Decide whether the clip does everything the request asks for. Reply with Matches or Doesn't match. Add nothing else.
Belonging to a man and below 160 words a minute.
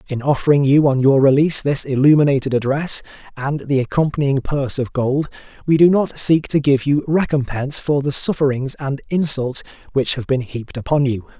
Doesn't match